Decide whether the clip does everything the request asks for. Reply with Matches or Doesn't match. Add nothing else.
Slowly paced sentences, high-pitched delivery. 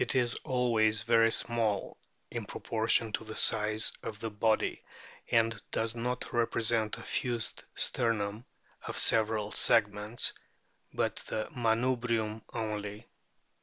Doesn't match